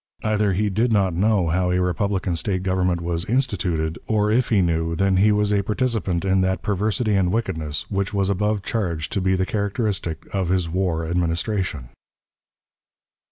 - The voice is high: No, very low, 95 Hz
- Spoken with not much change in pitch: No, average, 3.1 semitones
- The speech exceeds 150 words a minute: Yes, average, 170 wpm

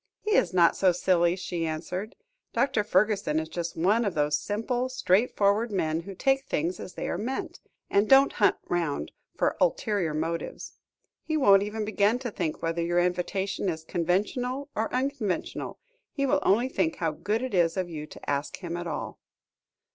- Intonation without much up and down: No, average, 5.2 semitones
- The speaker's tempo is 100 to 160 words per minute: No, average, 175 wpm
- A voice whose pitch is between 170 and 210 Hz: Yes, high, 190 Hz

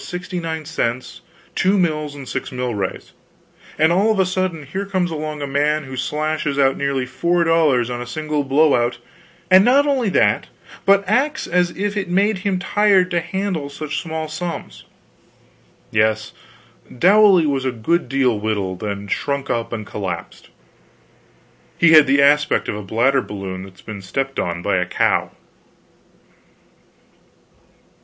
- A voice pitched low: No, medium, 150 Hz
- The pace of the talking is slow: No, average, 160 wpm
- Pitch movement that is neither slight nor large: No, wide, 6.6 semitones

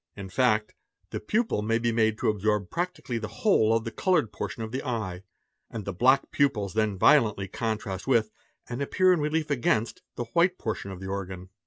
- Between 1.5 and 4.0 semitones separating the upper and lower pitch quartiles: No, average, 4.5 semitones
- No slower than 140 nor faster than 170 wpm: No, average, 200 wpm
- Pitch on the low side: Yes, low, 110 Hz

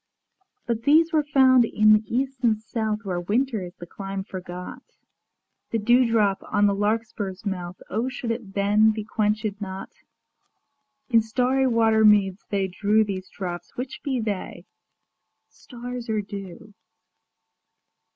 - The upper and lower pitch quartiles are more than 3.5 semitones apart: No, average, 3.2 semitones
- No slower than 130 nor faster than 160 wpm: Yes, average, 140 wpm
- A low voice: No, high, 215 Hz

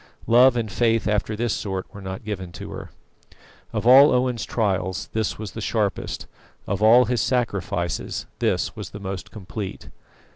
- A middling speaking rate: Yes, average, 160 wpm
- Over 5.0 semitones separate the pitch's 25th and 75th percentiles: No, average, 3.8 semitones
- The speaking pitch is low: Yes, low, 105 Hz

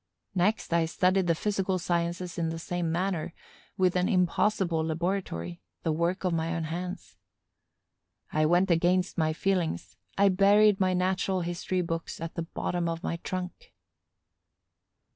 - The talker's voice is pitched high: No, medium, 175 Hz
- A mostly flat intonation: Yes, narrow, 2.0 semitones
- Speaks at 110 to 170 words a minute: Yes, average, 145 wpm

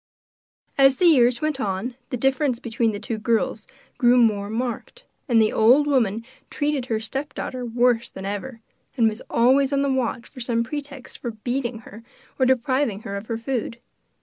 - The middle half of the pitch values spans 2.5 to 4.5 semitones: Yes, average, 3.0 semitones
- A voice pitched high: Yes, high, 240 Hz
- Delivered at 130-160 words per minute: No, average, 175 wpm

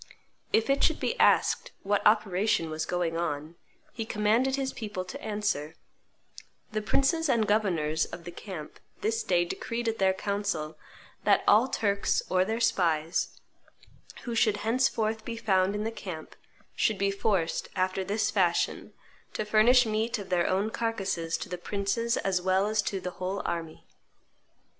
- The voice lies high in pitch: Yes, high, 205 Hz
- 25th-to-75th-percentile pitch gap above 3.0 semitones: Yes, average, 3.5 semitones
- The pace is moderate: Yes, average, 160 wpm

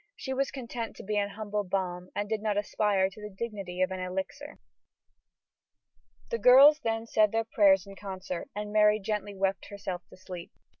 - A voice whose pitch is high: Yes, high, 205 Hz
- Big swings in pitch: No, narrow, 2.5 semitones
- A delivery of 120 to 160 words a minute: No, average, 185 wpm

